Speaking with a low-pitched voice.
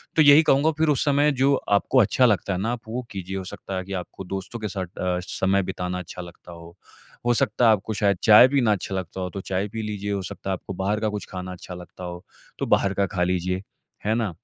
Yes: low, 100 Hz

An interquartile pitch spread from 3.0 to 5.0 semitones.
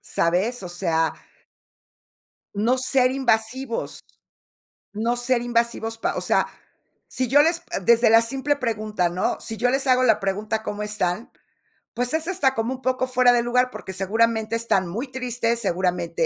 Yes: average, 3.3 semitones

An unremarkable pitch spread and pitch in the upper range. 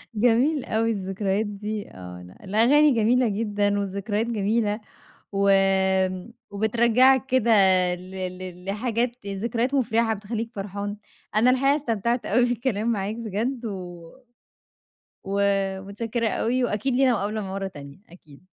Yes: average, 3.1 semitones; high, 215 Hz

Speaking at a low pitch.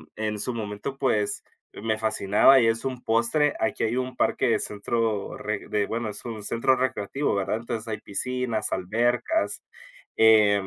Yes: low, 115 Hz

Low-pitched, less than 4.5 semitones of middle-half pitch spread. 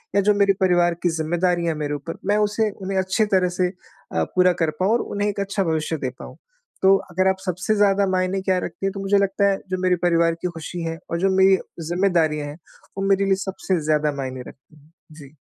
No: medium, 185 Hz; average, 3.0 semitones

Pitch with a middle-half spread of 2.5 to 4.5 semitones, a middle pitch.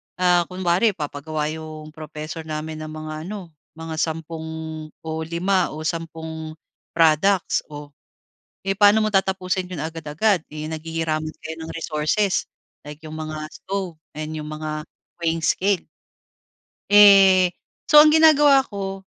Yes: average, 3.5 semitones; medium, 160 Hz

